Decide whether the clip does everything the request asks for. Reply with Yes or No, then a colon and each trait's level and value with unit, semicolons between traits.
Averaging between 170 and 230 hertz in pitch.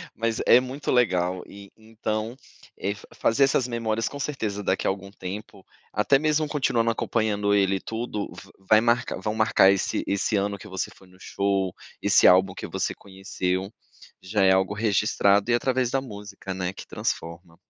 No: low, 105 Hz